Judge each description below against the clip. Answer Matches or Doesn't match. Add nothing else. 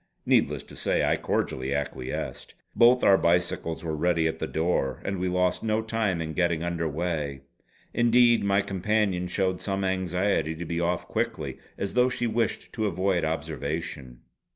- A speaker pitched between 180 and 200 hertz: Doesn't match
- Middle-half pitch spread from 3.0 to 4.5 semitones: Matches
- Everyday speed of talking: Matches